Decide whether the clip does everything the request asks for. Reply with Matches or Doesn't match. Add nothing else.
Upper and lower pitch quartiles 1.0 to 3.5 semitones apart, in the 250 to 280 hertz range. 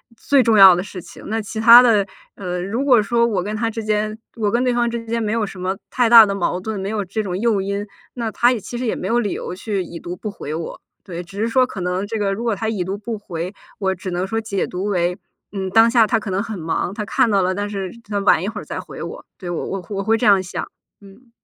Doesn't match